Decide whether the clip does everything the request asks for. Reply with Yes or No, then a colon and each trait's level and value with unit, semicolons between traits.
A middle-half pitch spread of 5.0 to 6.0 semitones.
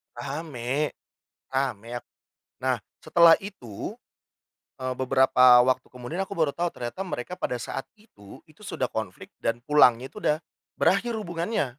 Yes: wide, 5.6 semitones